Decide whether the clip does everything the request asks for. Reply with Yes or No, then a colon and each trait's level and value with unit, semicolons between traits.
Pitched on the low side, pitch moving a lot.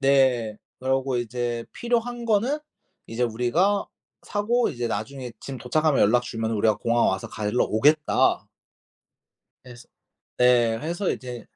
No: low, 125 Hz; average, 5.0 semitones